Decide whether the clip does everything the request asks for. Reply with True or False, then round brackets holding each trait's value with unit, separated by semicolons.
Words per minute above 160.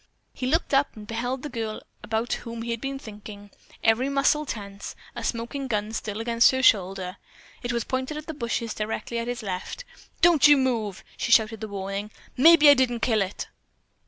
True (190 wpm)